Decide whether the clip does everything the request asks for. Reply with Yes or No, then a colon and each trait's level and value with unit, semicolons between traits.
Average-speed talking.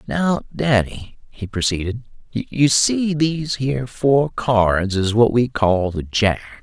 Yes: average, 145 wpm